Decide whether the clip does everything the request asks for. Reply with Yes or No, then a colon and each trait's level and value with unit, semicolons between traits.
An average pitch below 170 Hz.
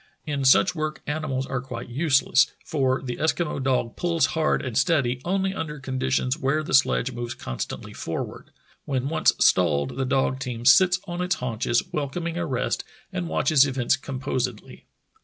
Yes: low, 135 Hz